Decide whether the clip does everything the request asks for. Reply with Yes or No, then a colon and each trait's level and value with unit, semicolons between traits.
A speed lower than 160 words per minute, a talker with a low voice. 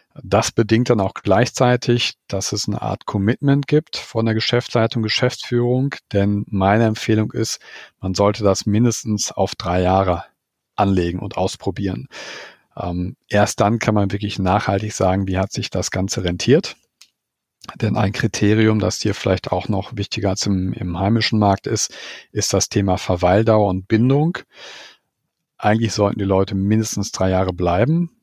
Yes: average, 150 wpm; low, 105 Hz